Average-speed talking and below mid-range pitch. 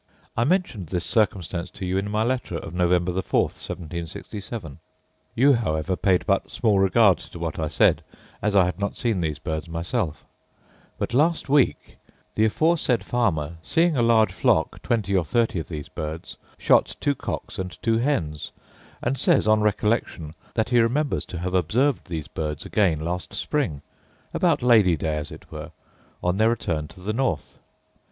Yes: average, 175 wpm; very low, 95 Hz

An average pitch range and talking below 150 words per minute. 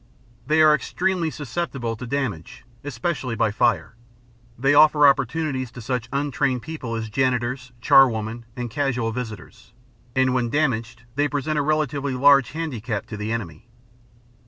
Yes: average, 3.9 semitones; average, 140 wpm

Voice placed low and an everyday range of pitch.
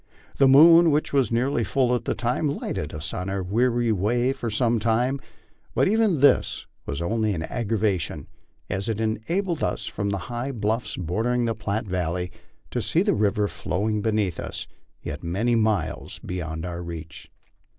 Yes: low, 110 Hz; average, 4.9 semitones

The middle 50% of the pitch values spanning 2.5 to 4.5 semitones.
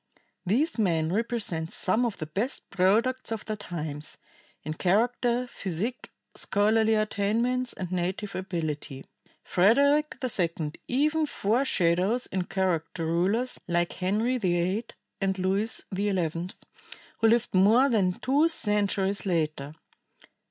No: average, 5.0 semitones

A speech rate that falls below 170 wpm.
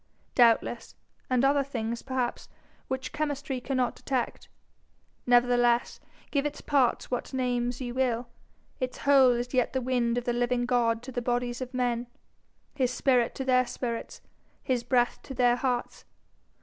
Yes: average, 150 wpm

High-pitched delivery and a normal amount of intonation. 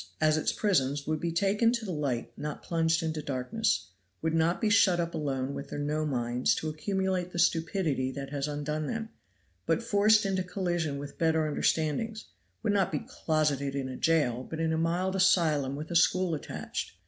No: medium, 160 Hz; average, 4.3 semitones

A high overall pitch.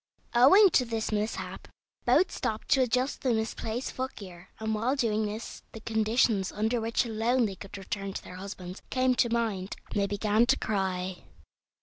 Yes: high, 220 Hz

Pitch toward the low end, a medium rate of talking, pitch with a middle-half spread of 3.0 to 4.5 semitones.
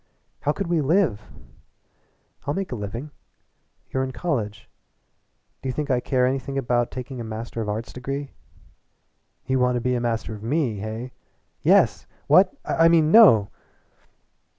Yes: low, 125 Hz; average, 150 wpm; average, 3.8 semitones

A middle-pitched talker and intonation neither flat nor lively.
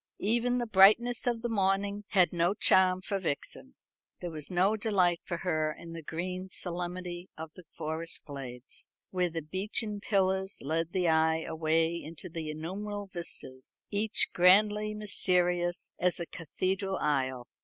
Yes: medium, 180 Hz; average, 3.5 semitones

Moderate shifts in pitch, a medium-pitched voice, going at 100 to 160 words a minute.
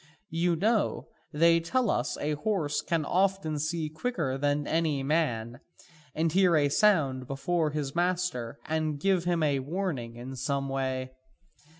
Yes: average, 4.2 semitones; medium, 155 Hz; average, 140 wpm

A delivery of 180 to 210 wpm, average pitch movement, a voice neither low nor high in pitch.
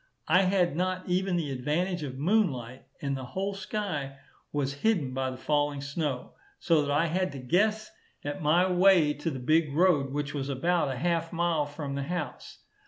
Yes: average, 185 wpm; average, 4.5 semitones; medium, 155 Hz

